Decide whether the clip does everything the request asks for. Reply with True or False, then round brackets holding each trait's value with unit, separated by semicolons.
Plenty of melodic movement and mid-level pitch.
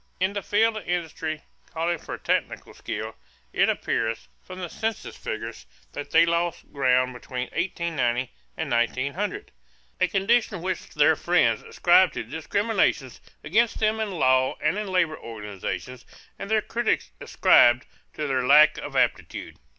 True (7.0 semitones; 165 Hz)